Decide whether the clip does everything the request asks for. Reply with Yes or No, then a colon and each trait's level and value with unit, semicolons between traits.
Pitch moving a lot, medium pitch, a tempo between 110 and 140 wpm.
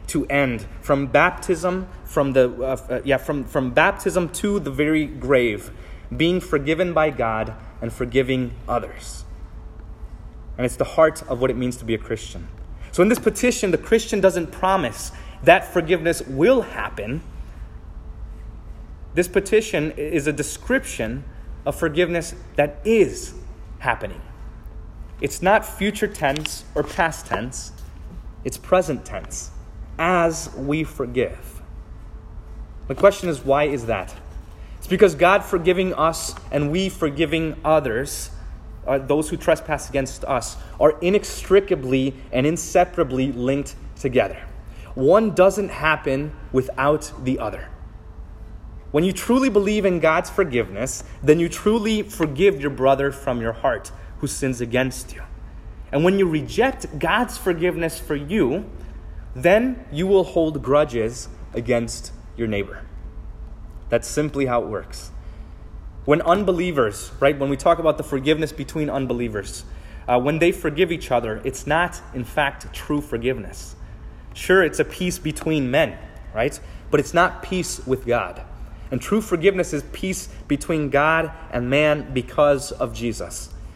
Yes: wide, 7.0 semitones; medium, 145 Hz; slow, 135 wpm